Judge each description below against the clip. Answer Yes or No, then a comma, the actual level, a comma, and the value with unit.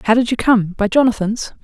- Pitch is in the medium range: No, high, 225 Hz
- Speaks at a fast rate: Yes, fast, 220 wpm